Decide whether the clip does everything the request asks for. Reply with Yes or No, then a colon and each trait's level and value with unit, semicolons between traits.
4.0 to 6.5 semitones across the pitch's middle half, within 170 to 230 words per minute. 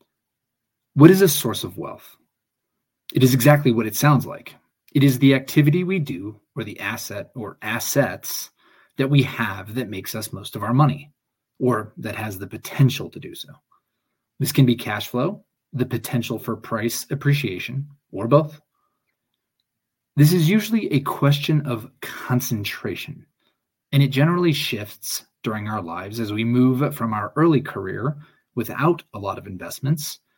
No: average, 4.3 semitones; average, 160 wpm